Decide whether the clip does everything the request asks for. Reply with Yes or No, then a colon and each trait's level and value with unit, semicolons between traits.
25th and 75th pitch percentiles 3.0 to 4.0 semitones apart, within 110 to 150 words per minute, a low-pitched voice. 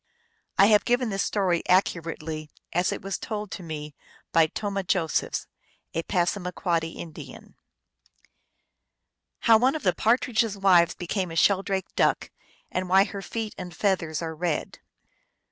No: average, 3.5 semitones; average, 145 wpm; medium, 185 Hz